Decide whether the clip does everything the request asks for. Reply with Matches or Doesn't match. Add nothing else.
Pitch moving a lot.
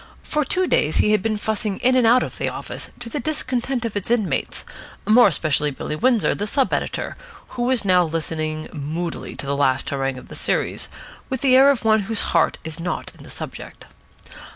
Matches